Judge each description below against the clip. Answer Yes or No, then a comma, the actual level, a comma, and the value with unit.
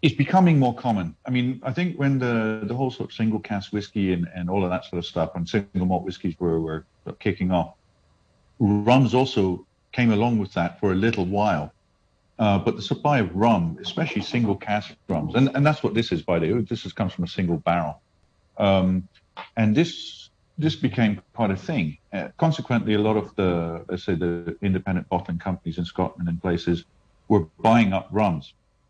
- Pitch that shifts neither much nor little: Yes, average, 4.7 semitones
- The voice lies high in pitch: No, low, 105 Hz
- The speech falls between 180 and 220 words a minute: Yes, average, 200 wpm